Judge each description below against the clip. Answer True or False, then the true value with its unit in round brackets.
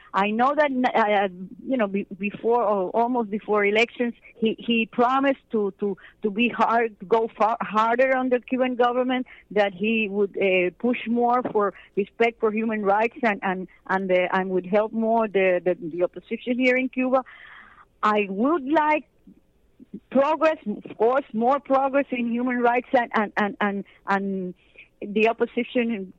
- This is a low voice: False (225 Hz)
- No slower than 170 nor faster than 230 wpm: False (155 wpm)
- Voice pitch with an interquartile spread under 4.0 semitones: True (3.6 semitones)